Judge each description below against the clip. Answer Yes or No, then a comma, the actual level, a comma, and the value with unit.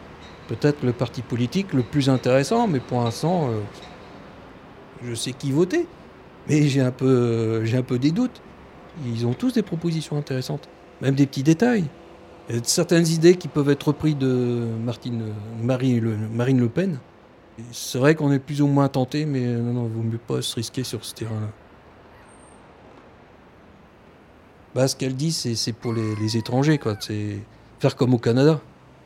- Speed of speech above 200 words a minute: No, average, 180 wpm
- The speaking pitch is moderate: No, low, 130 Hz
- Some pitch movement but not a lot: Yes, average, 4.2 semitones